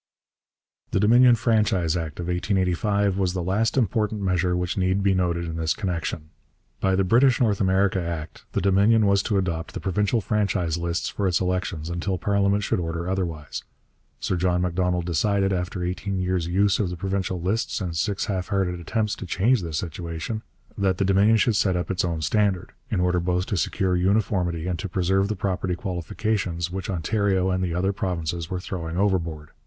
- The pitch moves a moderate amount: No, narrow, 2.3 semitones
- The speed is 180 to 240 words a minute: Yes, average, 185 wpm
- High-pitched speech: No, very low, 95 Hz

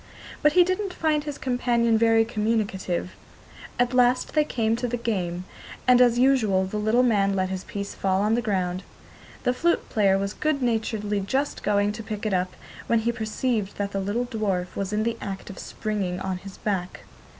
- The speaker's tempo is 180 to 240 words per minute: Yes, average, 195 wpm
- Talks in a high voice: Yes, high, 215 Hz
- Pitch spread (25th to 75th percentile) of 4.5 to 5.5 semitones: No, average, 3.7 semitones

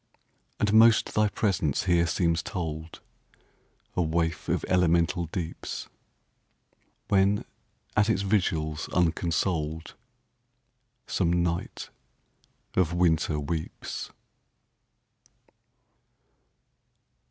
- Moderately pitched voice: No, very low, 85 Hz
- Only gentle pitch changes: No, average, 4.5 semitones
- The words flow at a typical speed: No, slow, 65 wpm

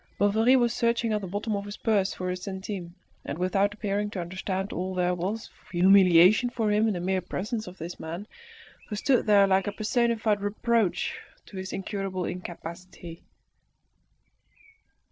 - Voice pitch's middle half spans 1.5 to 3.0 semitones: Yes, average, 2.7 semitones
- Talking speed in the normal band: Yes, average, 165 wpm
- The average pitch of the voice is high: Yes, high, 195 Hz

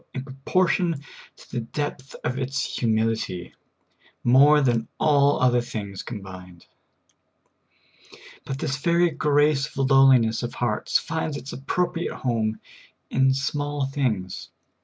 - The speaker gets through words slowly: Yes, slow, 120 wpm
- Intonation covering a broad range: No, average, 4.3 semitones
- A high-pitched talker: No, low, 135 Hz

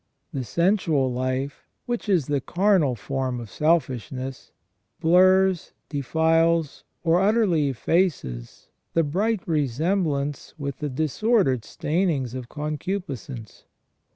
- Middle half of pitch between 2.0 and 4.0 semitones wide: No, average, 5.3 semitones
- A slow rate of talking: Yes, slow, 105 wpm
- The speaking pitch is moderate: Yes, medium, 150 Hz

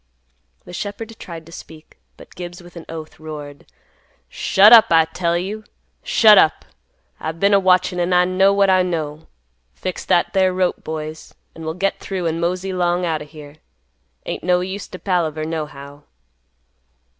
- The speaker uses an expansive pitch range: No, average, 2.8 semitones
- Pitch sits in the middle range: Yes, medium, 175 Hz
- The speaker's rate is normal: Yes, average, 170 wpm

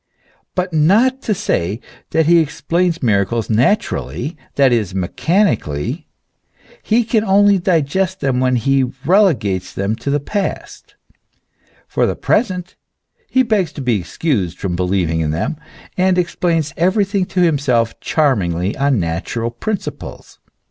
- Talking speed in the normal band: No, slow, 130 wpm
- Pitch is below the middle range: No, medium, 145 Hz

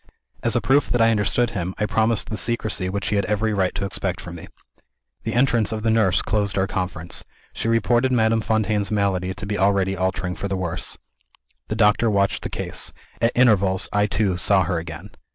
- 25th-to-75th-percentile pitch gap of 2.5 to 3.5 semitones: Yes, average, 2.9 semitones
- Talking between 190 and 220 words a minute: Yes, fast, 205 wpm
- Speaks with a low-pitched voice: Yes, low, 100 Hz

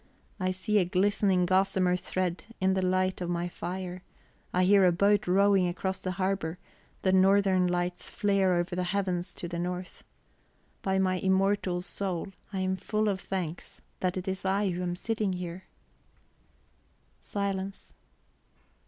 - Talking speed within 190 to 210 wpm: No, average, 155 wpm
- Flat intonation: Yes, narrow, 1.5 semitones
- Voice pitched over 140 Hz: Yes, medium, 185 Hz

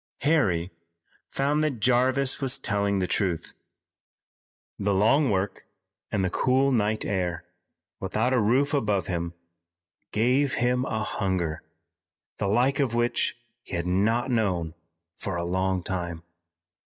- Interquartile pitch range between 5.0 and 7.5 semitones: Yes, wide, 5.5 semitones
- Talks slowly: Yes, slow, 130 wpm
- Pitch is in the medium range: No, low, 105 Hz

